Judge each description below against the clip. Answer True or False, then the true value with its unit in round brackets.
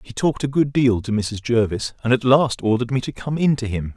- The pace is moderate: False (275 wpm)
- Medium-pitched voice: False (120 Hz)